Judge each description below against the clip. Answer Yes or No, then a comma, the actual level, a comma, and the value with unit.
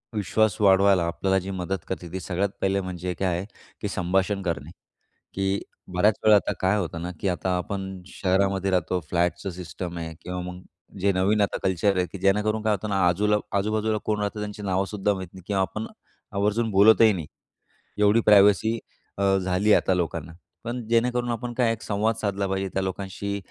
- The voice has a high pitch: No, very low, 95 Hz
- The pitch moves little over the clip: Yes, narrow, 2.3 semitones